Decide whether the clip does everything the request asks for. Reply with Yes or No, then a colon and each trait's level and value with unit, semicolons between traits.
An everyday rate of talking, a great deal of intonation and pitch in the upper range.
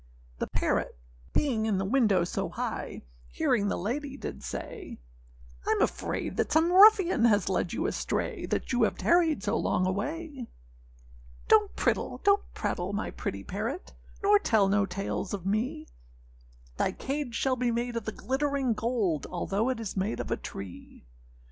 Yes: average, 160 wpm; wide, 6.5 semitones; high, 230 Hz